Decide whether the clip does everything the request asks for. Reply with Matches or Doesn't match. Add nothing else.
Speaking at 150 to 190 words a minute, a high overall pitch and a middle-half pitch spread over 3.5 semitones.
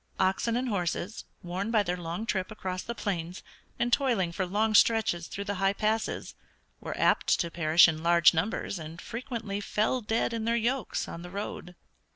Matches